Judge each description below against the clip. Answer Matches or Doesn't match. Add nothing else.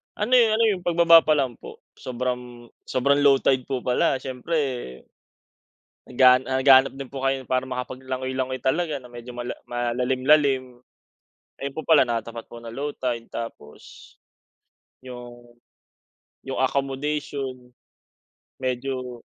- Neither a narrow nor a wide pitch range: Doesn't match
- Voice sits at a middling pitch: Doesn't match